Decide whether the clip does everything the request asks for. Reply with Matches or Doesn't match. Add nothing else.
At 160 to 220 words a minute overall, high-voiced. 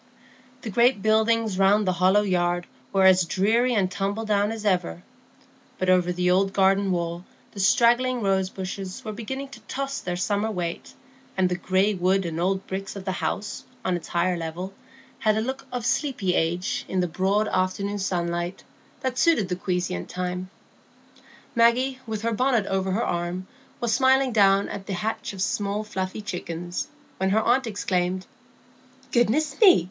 Matches